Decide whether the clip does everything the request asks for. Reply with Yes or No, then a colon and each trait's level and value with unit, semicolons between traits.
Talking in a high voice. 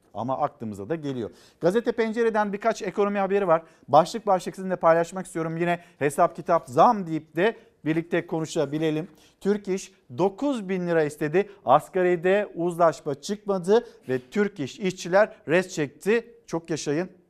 No: medium, 175 Hz